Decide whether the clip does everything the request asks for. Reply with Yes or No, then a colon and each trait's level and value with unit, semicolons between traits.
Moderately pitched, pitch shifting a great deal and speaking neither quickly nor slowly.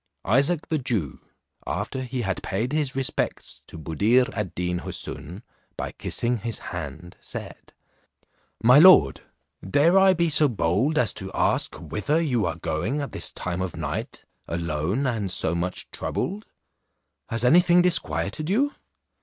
No: low, 120 Hz; wide, 8.7 semitones; average, 150 wpm